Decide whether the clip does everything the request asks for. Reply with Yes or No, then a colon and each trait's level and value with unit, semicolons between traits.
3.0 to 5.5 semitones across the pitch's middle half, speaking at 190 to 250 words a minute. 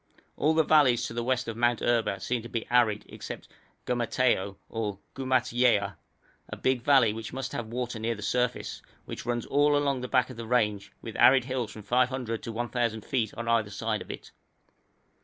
No: narrow, 2.4 semitones; average, 195 wpm